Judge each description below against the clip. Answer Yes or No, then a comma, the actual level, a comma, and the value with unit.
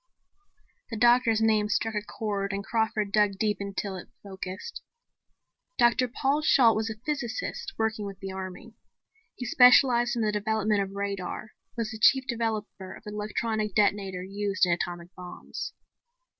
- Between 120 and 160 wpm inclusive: Yes, average, 155 wpm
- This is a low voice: No, high, 210 Hz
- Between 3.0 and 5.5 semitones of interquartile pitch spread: No, narrow, 2.5 semitones